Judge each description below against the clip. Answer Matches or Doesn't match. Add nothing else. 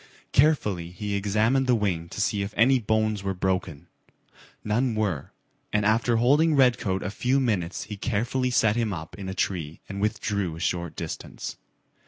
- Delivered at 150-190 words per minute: Matches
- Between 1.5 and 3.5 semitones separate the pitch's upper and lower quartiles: Doesn't match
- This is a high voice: Doesn't match